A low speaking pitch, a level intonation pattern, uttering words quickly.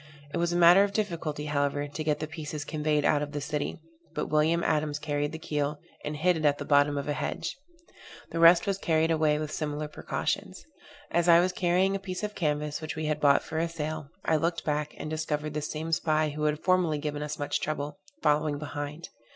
No: medium, 155 Hz; narrow, 2.0 semitones; fast, 220 wpm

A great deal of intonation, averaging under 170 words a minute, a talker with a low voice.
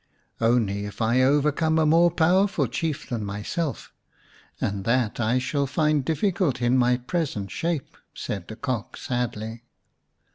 Yes: wide, 5.8 semitones; average, 145 wpm; low, 130 Hz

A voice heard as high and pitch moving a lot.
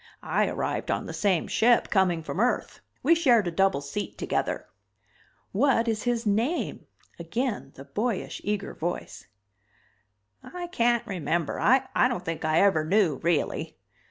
Yes: high, 205 Hz; wide, 6.3 semitones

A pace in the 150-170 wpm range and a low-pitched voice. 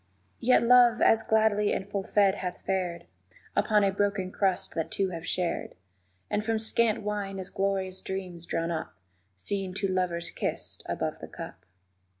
No: average, 160 wpm; high, 195 Hz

